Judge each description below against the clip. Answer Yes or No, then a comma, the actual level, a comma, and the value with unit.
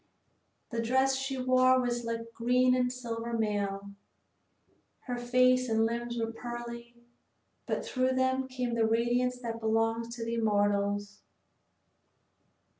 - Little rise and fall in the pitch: Yes, narrow, 1.9 semitones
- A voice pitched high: Yes, high, 235 Hz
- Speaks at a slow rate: Yes, slow, 125 wpm